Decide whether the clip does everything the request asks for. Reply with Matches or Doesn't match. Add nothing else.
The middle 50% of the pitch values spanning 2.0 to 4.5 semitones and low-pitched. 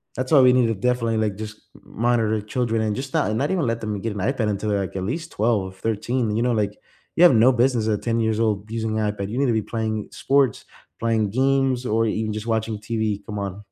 Matches